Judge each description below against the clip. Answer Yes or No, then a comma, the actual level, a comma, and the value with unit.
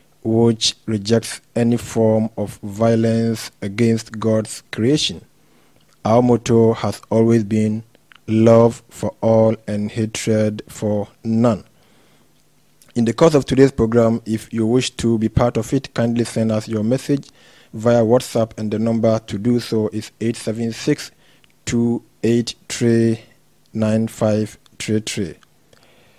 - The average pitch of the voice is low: Yes, low, 115 Hz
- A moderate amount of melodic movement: No, narrow, 1.4 semitones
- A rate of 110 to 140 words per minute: Yes, slow, 135 wpm